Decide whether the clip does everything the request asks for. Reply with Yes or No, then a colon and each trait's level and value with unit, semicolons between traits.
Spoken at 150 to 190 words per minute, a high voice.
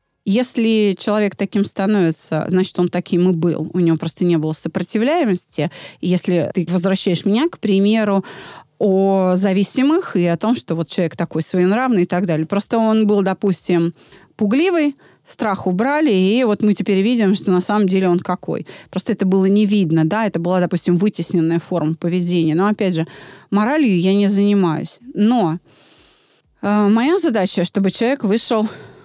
Yes: fast, 160 wpm; high, 195 Hz